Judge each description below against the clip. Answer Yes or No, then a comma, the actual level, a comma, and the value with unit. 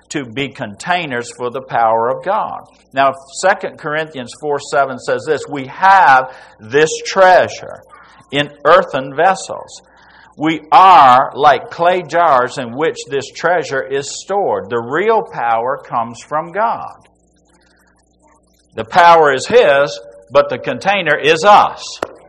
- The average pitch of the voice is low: No, medium, 150 Hz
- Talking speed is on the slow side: Yes, slow, 130 wpm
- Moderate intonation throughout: No, wide, 7.6 semitones